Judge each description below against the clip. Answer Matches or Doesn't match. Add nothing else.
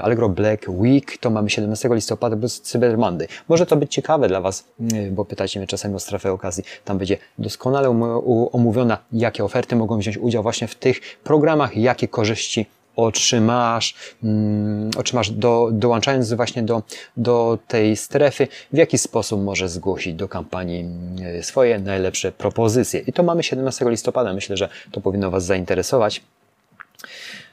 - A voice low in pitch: Matches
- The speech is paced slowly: Doesn't match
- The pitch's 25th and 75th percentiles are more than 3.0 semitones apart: Matches